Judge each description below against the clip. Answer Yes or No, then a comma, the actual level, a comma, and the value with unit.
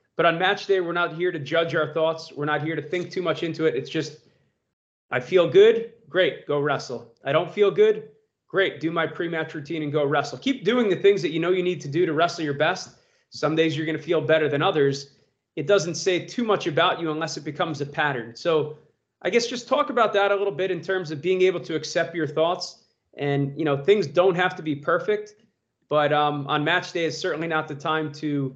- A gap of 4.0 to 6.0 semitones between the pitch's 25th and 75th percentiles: No, average, 3.4 semitones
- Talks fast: Yes, fast, 240 wpm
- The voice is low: No, medium, 165 Hz